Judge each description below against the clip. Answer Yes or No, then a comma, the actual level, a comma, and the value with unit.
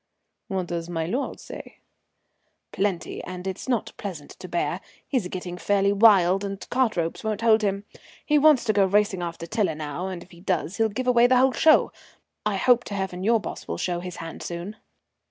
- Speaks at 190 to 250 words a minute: Yes, average, 200 wpm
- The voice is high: Yes, high, 195 Hz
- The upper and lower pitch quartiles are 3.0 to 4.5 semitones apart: Yes, average, 3.9 semitones